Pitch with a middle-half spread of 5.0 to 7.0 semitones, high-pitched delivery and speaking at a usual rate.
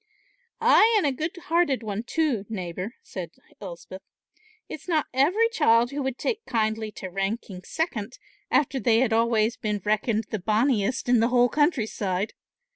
Yes: wide, 5.4 semitones; high, 235 Hz; average, 155 wpm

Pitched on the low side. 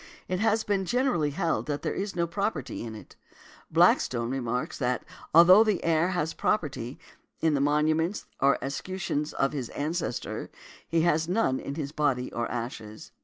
No: medium, 150 Hz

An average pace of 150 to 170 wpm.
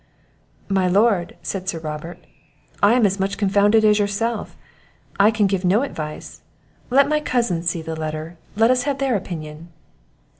Yes: average, 160 wpm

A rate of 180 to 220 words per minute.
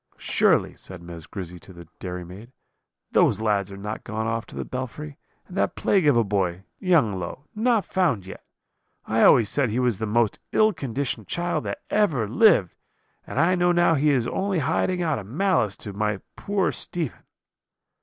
Yes: average, 185 wpm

